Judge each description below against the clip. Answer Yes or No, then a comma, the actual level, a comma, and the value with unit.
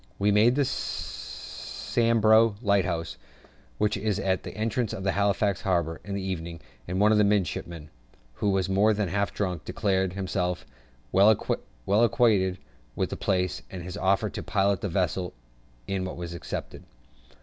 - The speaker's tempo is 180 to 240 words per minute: No, average, 150 wpm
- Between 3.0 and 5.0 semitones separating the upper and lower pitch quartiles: No, narrow, 2.5 semitones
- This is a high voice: No, very low, 95 Hz